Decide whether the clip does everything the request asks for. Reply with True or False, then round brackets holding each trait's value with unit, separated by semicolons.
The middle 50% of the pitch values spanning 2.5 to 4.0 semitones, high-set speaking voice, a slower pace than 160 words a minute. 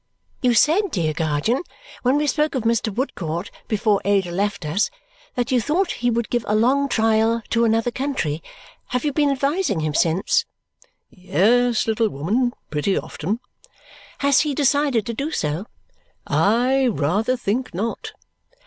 False (5.2 semitones; 230 Hz; 150 wpm)